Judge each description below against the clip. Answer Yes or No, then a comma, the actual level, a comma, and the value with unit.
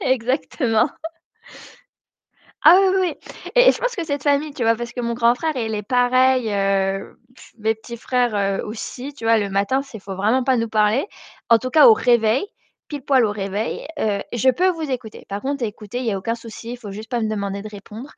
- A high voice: Yes, high, 235 Hz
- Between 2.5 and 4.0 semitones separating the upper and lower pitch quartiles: Yes, average, 3.7 semitones